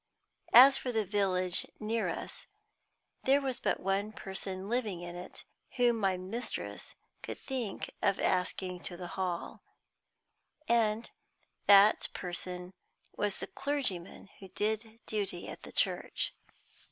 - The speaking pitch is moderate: No, high, 200 Hz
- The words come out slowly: Yes, slow, 130 wpm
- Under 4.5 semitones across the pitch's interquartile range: Yes, average, 3.7 semitones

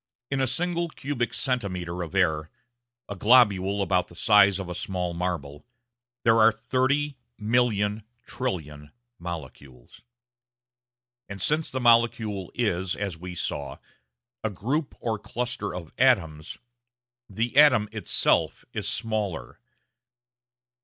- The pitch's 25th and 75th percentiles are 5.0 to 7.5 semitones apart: Yes, wide, 5.4 semitones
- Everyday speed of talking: No, slow, 120 wpm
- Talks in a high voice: No, low, 105 Hz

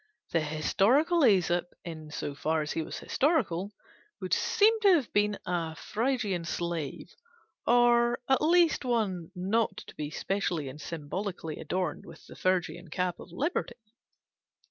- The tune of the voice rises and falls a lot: Yes, wide, 6.5 semitones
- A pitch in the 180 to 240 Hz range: Yes, medium, 185 Hz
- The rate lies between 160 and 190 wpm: No, average, 145 wpm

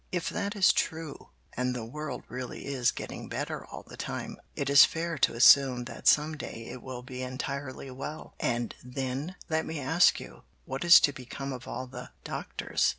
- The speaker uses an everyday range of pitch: Yes, average, 3.4 semitones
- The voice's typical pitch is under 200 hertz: Yes, low, 135 Hz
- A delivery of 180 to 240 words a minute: Yes, average, 190 wpm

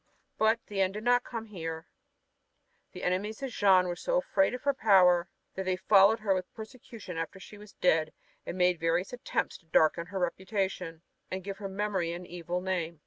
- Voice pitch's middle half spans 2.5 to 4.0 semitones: Yes, average, 3.3 semitones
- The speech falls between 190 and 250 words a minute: Yes, average, 195 wpm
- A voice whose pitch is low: No, high, 190 Hz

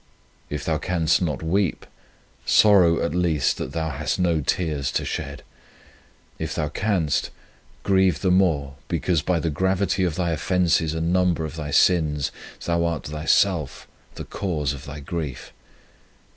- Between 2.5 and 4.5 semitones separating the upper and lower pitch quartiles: Yes, average, 3.3 semitones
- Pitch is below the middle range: Yes, very low, 80 Hz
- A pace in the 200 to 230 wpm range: No, average, 150 wpm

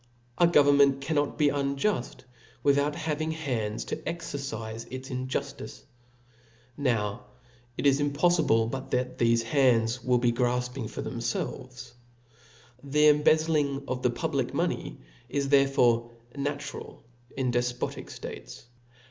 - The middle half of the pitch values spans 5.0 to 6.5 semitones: No, average, 2.9 semitones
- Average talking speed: No, slow, 115 wpm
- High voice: No, low, 135 Hz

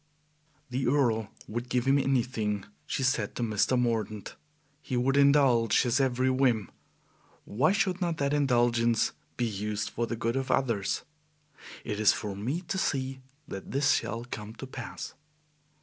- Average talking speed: Yes, average, 155 wpm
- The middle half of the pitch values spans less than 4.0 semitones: Yes, average, 3.5 semitones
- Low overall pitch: Yes, low, 120 Hz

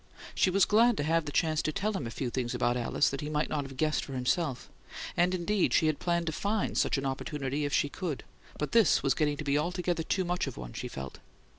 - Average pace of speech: No, fast, 250 wpm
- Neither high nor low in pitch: Yes, medium, 150 Hz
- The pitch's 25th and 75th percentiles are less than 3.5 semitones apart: No, average, 4.5 semitones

